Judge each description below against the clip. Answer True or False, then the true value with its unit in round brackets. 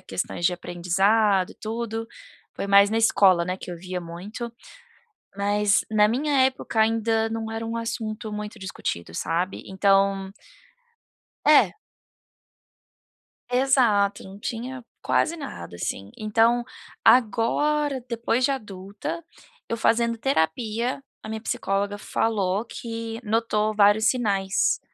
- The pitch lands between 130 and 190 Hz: False (215 Hz)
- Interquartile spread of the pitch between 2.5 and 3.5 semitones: True (2.9 semitones)